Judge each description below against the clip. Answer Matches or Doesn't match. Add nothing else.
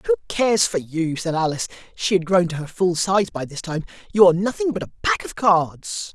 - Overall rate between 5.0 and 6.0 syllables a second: Doesn't match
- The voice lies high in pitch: Doesn't match